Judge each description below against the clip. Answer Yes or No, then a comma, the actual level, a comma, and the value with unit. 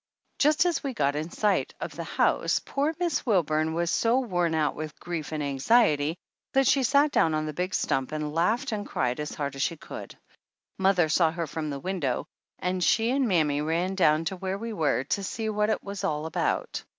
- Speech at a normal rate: No, fast, 210 wpm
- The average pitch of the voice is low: No, medium, 175 Hz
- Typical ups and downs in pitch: No, wide, 5.9 semitones